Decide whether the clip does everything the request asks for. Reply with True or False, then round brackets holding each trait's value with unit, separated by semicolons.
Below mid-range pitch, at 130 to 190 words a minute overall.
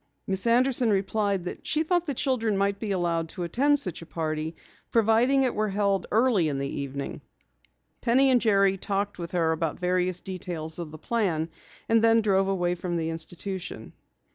False (195 Hz; 180 wpm)